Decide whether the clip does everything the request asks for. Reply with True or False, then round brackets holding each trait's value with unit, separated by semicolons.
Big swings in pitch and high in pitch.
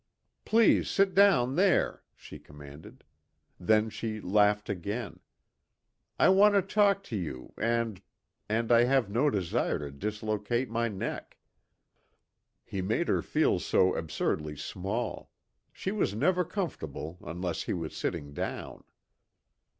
False (8.0 semitones; 110 Hz)